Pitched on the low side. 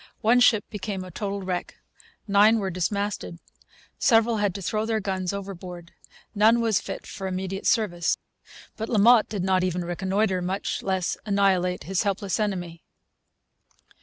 No: high, 195 Hz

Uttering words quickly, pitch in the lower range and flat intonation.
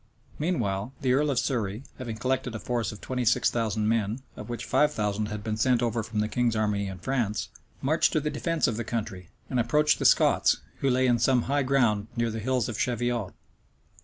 No: fast, 215 wpm; low, 120 Hz; average, 3.4 semitones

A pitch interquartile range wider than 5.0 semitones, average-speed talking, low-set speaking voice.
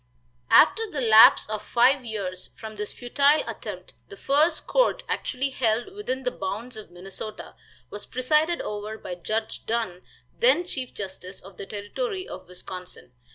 No: wide, 5.6 semitones; average, 155 wpm; high, 225 Hz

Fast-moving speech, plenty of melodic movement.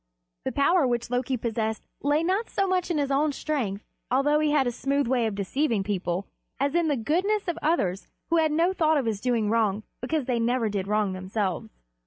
Yes: fast, 210 wpm; wide, 6.1 semitones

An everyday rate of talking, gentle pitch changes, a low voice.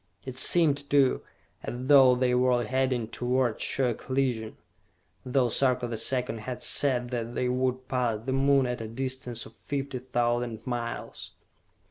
Yes: average, 150 wpm; narrow, 1.5 semitones; low, 125 Hz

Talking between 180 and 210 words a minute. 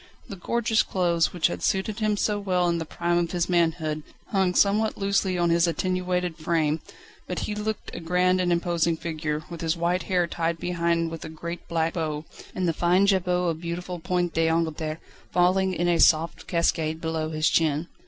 Yes: average, 190 wpm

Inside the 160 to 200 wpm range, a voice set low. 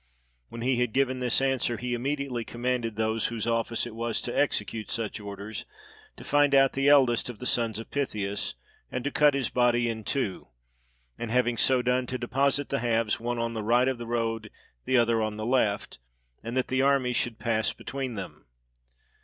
Yes: average, 195 wpm; low, 120 Hz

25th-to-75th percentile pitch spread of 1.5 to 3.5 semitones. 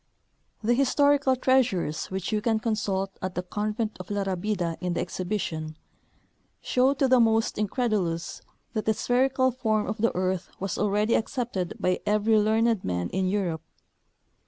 No: average, 4.0 semitones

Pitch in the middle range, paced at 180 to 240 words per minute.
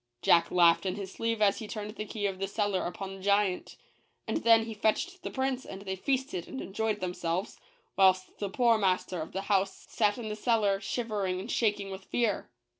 No: high, 205 Hz; fast, 205 wpm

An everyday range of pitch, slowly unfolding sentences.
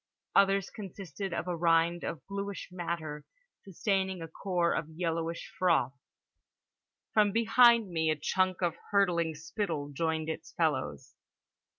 Yes: average, 3.4 semitones; slow, 125 wpm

